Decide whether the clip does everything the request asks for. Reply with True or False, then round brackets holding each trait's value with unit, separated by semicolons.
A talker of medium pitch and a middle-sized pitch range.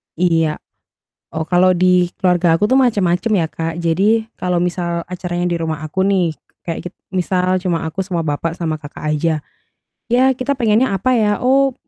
True (180 Hz; 3.2 semitones)